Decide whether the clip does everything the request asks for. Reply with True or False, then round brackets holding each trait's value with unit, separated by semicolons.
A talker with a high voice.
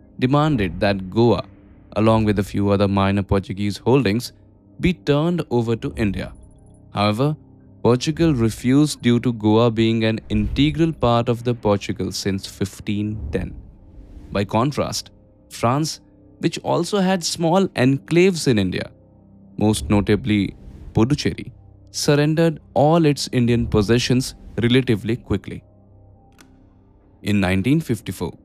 False (105 Hz)